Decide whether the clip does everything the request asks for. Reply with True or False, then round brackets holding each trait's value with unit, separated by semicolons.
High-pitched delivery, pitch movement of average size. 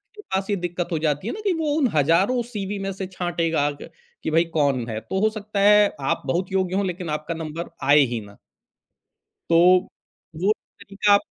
False (180 Hz; 4.7 semitones)